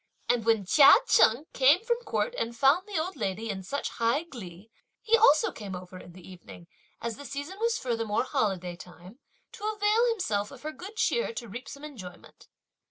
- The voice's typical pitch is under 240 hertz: No, very high, 255 Hz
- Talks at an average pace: Yes, average, 190 wpm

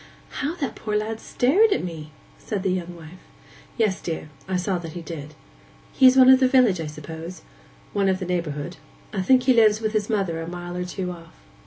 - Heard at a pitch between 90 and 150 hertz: No, medium, 185 Hz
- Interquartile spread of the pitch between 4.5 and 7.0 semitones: Yes, average, 4.8 semitones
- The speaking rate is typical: No, fast, 215 wpm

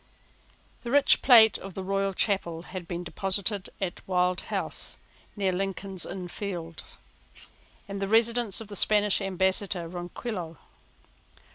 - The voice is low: No, high, 195 Hz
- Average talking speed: No, slow, 125 wpm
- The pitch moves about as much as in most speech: No, narrow, 2.3 semitones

